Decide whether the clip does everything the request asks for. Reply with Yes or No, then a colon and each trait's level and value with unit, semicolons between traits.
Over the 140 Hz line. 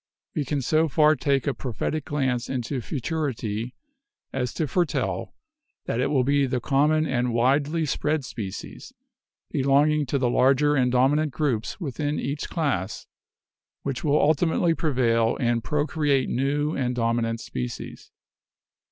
No: low, 135 Hz